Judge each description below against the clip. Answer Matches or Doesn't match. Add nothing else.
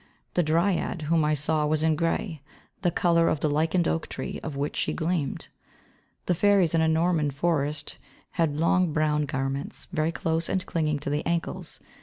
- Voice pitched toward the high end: Doesn't match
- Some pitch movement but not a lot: Doesn't match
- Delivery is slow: Doesn't match